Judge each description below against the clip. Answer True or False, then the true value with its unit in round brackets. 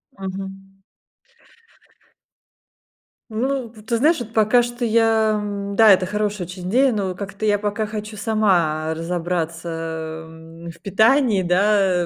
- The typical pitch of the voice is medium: False (200 Hz)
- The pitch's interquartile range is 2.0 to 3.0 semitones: False (3.7 semitones)